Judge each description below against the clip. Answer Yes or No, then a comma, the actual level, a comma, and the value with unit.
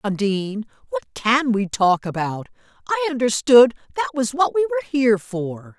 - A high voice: Yes, high, 240 Hz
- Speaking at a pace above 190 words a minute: No, average, 145 wpm